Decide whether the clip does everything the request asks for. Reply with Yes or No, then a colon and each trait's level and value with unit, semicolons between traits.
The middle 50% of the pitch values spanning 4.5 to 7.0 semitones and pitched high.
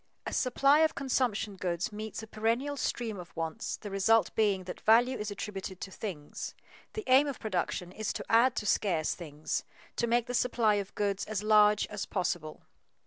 No: average, 3.9 semitones; high, 210 Hz